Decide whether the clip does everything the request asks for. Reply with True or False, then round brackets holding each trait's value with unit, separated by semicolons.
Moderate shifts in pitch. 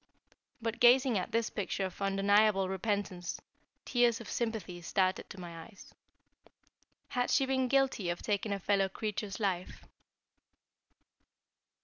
True (3.5 semitones)